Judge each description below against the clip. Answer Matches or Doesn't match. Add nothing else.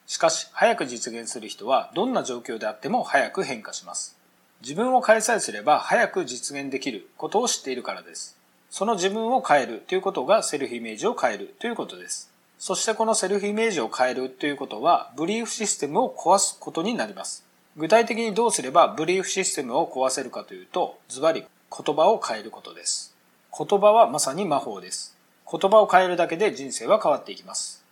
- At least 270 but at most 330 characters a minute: Doesn't match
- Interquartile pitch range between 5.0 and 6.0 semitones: Doesn't match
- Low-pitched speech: Doesn't match